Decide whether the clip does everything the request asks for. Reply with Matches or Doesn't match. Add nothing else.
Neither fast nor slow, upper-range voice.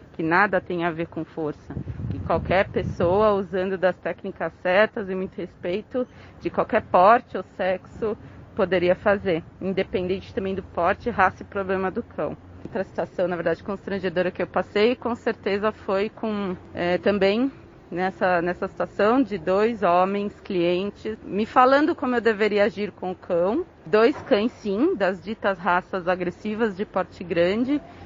Matches